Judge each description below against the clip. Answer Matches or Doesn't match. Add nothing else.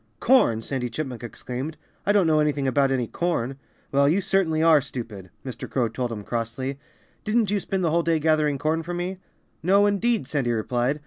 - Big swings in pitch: Matches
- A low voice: Doesn't match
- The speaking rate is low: Doesn't match